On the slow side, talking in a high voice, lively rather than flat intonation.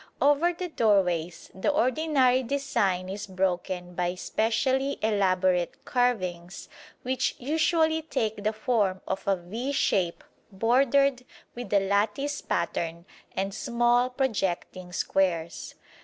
Yes: slow, 110 wpm; high, 215 Hz; wide, 6.0 semitones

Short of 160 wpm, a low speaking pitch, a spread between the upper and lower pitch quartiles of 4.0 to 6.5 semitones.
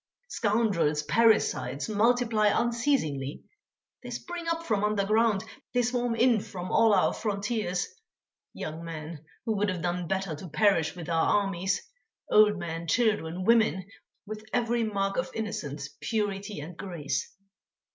No: slow, 135 wpm; high, 200 Hz; average, 4.7 semitones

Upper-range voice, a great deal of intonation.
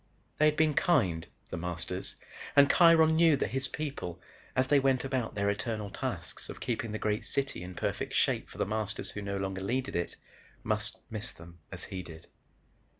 No: low, 110 Hz; wide, 6.5 semitones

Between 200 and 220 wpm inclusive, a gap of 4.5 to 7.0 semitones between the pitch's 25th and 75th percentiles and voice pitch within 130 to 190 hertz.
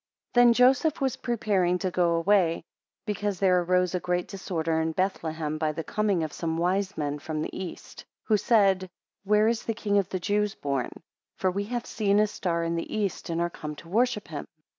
No: fast, 205 wpm; average, 3.9 semitones; medium, 185 Hz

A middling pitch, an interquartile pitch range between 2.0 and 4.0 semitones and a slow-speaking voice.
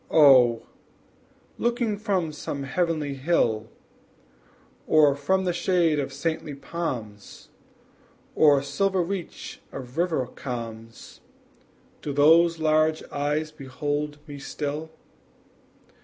Yes: medium, 150 Hz; average, 3.5 semitones; slow, 95 wpm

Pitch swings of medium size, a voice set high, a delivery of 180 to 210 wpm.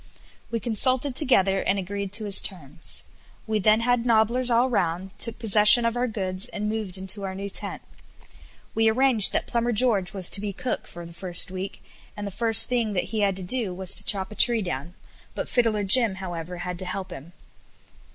Yes: average, 3.6 semitones; high, 205 Hz; average, 200 wpm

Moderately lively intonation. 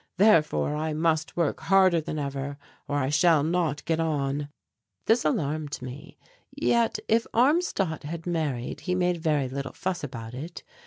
Yes: average, 3.6 semitones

